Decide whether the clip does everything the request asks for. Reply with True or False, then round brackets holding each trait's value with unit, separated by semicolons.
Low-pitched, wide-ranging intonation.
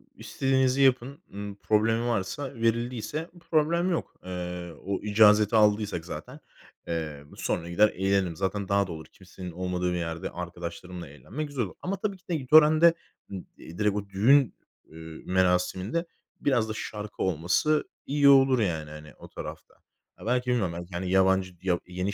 True (100 Hz; 6.2 semitones)